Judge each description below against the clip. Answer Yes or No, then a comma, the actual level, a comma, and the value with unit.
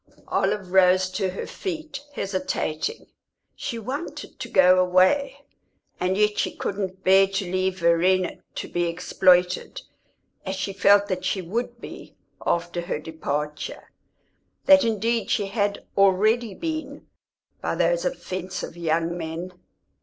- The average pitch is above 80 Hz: Yes, high, 190 Hz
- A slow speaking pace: Yes, slow, 130 wpm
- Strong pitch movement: No, average, 3.2 semitones